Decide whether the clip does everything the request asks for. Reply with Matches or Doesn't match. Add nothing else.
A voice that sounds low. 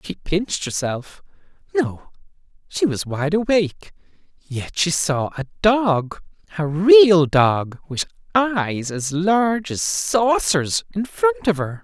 Doesn't match